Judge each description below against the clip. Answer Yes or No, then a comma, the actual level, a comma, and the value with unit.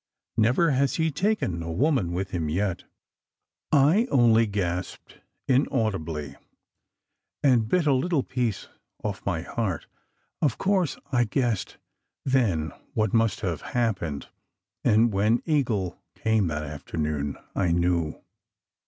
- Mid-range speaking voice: No, low, 110 Hz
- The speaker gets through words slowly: Yes, slow, 125 wpm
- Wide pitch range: Yes, wide, 7.2 semitones